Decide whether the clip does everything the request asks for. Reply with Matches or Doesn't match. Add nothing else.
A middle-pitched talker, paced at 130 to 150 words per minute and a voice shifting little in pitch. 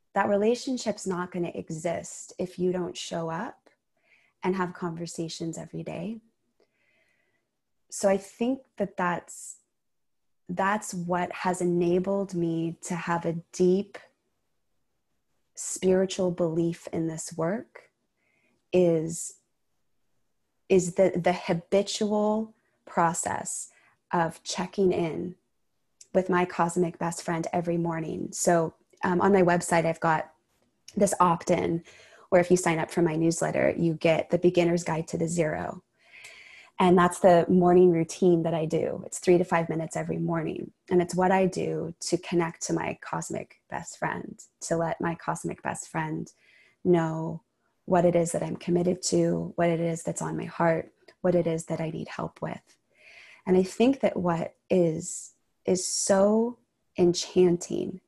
Matches